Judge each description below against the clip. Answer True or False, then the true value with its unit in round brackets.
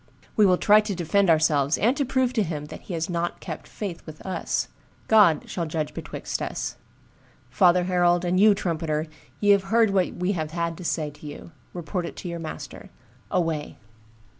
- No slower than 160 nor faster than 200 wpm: True (190 wpm)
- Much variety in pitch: False (3.7 semitones)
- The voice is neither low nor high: True (175 Hz)